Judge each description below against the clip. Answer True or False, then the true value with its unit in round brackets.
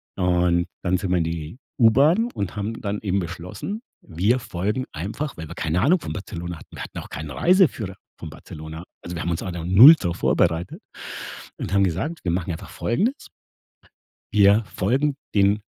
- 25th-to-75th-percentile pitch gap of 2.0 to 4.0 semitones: False (5.5 semitones)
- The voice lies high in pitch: False (95 Hz)